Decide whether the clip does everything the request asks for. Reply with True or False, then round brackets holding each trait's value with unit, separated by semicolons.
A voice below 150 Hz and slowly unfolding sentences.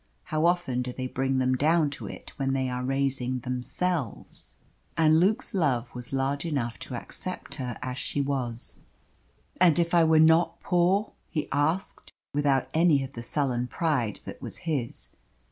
False (140 Hz; 165 wpm)